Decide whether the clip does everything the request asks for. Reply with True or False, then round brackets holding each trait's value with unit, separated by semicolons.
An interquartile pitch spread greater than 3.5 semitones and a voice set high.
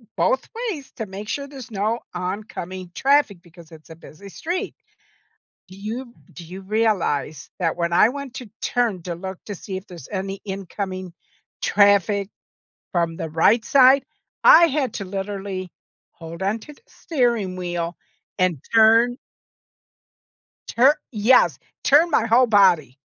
True (4.8 semitones; 200 Hz)